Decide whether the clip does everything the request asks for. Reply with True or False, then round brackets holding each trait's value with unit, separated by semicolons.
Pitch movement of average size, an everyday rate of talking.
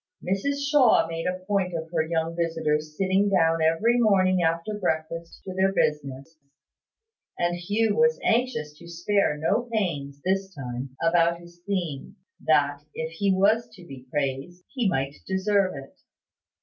True (3.9 semitones; 150 wpm)